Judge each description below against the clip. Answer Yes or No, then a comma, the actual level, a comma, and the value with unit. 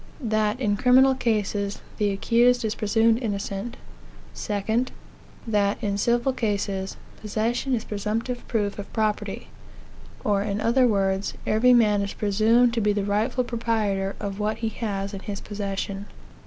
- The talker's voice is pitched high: Yes, high, 210 Hz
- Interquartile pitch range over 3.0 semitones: No, narrow, 2.5 semitones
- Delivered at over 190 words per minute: No, average, 145 wpm